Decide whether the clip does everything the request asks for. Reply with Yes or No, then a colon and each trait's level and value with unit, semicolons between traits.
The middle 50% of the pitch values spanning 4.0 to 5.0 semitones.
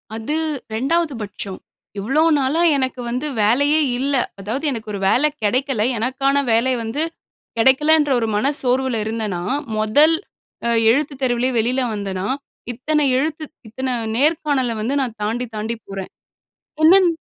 Yes: average, 4.4 semitones